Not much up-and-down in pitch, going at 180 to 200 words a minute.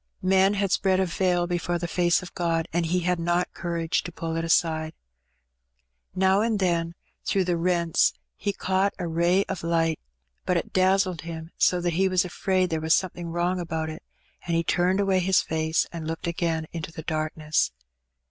Yes: narrow, 2.1 semitones; average, 190 wpm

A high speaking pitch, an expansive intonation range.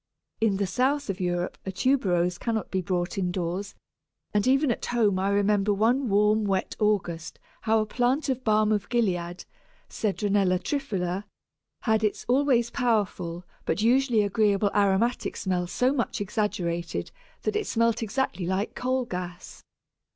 No: high, 210 Hz; average, 4.2 semitones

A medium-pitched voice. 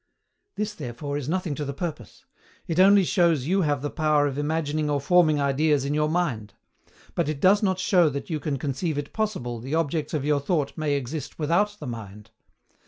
Yes: medium, 150 Hz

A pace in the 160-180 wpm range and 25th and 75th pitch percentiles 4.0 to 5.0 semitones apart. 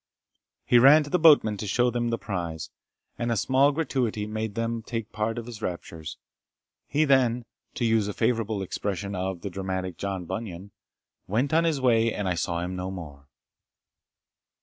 Yes: average, 175 wpm; average, 4.4 semitones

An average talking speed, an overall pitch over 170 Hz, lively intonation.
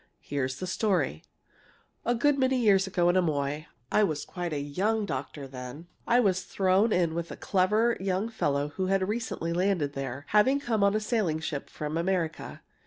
Yes: average, 180 wpm; medium, 185 Hz; wide, 6.0 semitones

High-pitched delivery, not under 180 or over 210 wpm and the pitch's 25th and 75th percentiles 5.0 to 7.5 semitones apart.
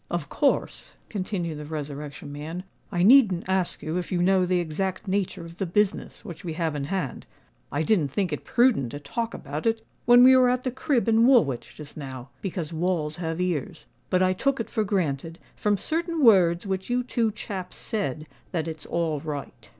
No: medium, 180 Hz; average, 195 wpm; wide, 5.5 semitones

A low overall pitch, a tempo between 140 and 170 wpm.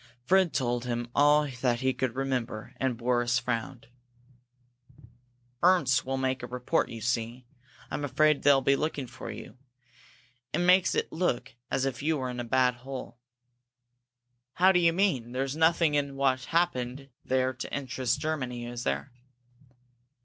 Yes: low, 130 Hz; average, 160 wpm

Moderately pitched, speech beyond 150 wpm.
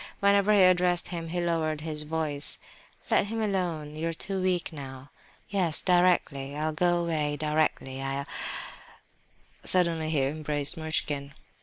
No: medium, 160 Hz; slow, 135 wpm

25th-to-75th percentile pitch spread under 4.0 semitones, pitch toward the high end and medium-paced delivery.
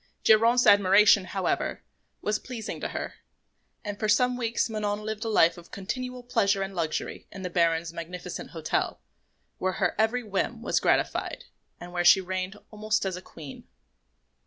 Yes: average, 3.4 semitones; high, 200 Hz; average, 160 wpm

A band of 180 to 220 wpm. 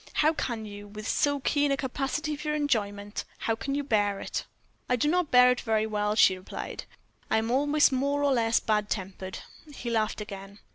Yes: average, 195 wpm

